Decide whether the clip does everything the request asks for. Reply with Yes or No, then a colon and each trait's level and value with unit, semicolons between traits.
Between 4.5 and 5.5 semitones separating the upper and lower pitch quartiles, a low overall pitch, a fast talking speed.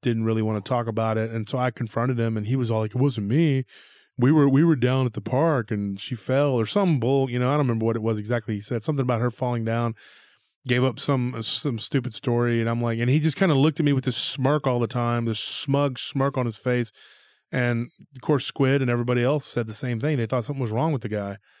No: average, 3.1 semitones; low, 125 Hz; fast, 270 wpm